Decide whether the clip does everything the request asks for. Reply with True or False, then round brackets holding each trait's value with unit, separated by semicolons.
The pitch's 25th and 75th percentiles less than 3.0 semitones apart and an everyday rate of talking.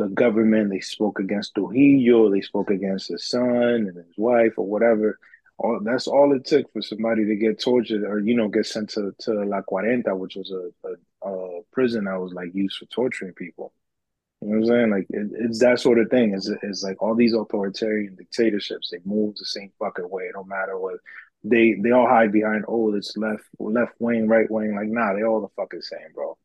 False (2.6 semitones; 215 wpm)